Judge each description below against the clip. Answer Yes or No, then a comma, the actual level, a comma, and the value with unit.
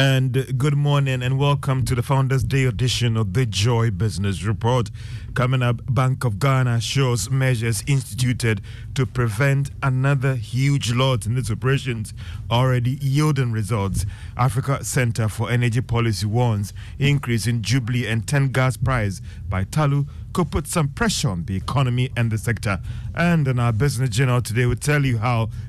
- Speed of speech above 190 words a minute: No, average, 165 wpm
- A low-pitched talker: Yes, low, 125 Hz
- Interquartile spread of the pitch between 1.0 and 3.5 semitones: Yes, average, 3.1 semitones